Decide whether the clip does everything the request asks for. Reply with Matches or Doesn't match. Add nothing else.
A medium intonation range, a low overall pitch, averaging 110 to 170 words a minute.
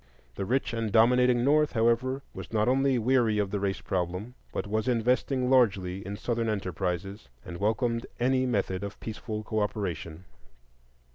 Matches